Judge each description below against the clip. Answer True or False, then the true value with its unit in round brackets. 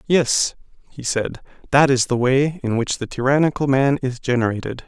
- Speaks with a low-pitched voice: True (130 Hz)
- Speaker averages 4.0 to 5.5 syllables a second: True (5.0 syllables/s)